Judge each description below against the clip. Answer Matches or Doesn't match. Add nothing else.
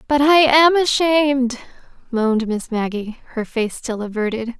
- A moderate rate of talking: Matches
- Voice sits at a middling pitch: Doesn't match